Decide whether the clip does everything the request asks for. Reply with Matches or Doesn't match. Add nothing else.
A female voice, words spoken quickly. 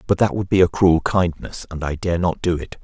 Doesn't match